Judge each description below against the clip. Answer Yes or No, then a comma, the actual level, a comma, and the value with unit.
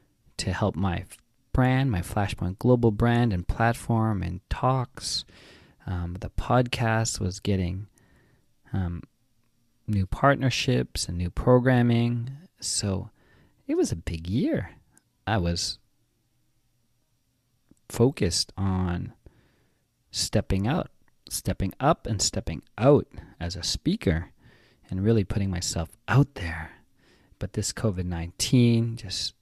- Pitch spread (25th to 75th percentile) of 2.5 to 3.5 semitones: No, average, 4.7 semitones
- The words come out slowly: Yes, slow, 110 wpm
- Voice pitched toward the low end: Yes, low, 105 Hz